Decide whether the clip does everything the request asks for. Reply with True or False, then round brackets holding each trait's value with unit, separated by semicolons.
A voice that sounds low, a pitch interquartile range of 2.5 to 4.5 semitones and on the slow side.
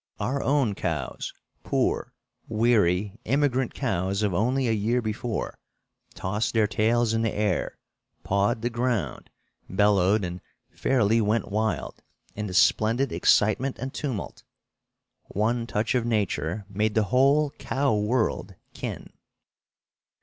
True (110 Hz; 3.0 semitones; 125 wpm)